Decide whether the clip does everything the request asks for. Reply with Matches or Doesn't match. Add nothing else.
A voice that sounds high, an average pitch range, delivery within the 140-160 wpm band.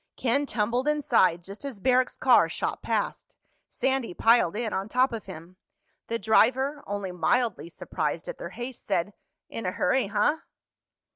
Matches